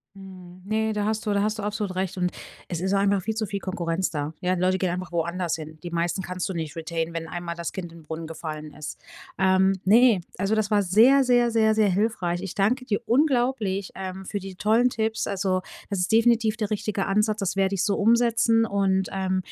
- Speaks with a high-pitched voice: Yes, high, 195 Hz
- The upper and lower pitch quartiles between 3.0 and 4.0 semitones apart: Yes, average, 3.4 semitones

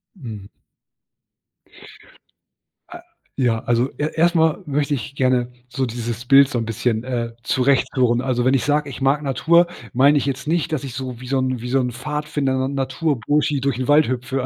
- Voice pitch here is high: No, low, 130 Hz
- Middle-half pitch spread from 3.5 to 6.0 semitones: No, average, 2.9 semitones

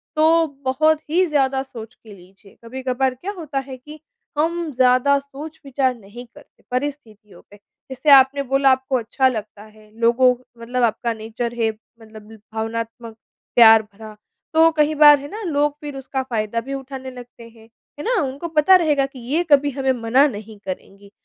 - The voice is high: Yes, very high, 260 Hz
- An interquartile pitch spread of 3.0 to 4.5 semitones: Yes, average, 4.2 semitones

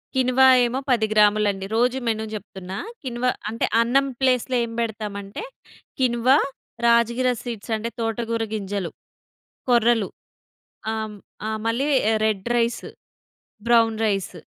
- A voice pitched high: Yes, high, 230 Hz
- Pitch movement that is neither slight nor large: No, narrow, 2.2 semitones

